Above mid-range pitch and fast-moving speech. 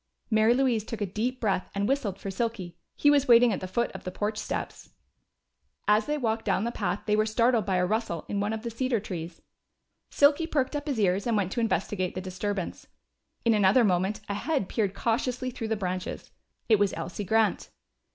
Yes: high, 215 Hz; fast, 210 wpm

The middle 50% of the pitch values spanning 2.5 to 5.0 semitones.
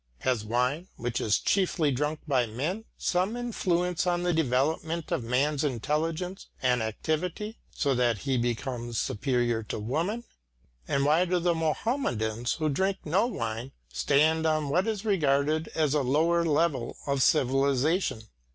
No: wide, 5.4 semitones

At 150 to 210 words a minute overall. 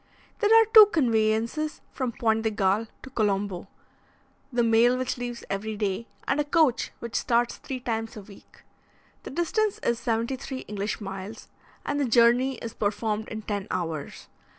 Yes: average, 165 wpm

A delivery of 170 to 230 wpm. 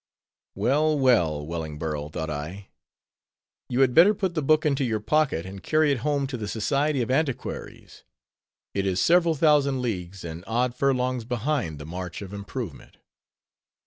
No: average, 155 wpm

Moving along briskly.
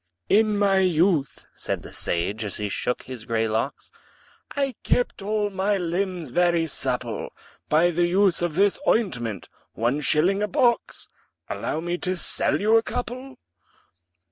No: average, 150 wpm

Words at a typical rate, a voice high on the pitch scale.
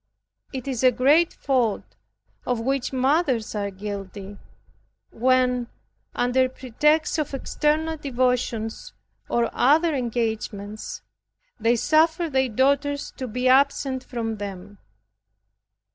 No: slow, 105 wpm; very high, 255 Hz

